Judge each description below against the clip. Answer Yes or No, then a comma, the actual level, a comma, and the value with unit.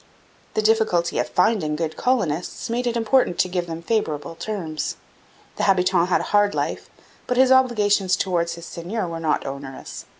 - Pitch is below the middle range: No, medium, 185 Hz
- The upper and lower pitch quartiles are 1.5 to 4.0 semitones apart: No, average, 4.9 semitones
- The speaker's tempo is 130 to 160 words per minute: No, average, 170 wpm